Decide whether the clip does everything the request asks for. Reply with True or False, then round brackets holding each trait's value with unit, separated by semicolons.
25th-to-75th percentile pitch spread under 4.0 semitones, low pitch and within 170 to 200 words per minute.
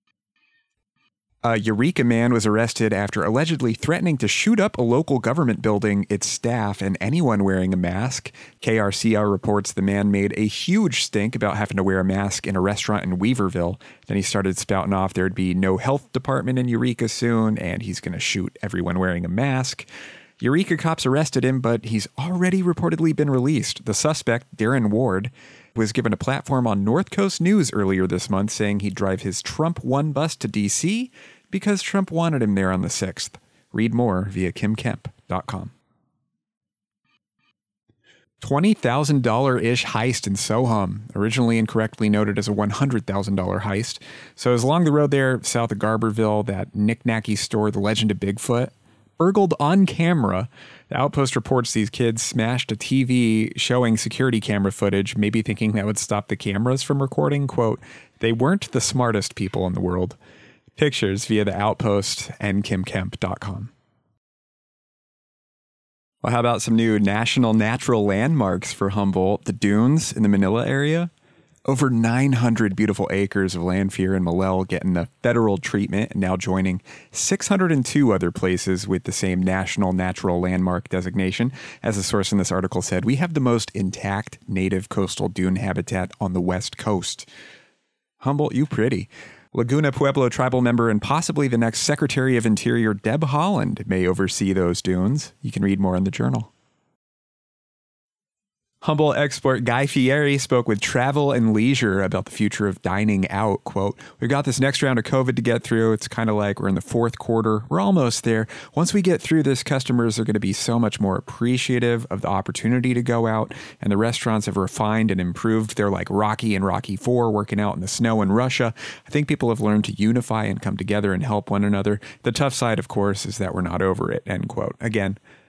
False (4.6 semitones; 110 Hz; 180 wpm)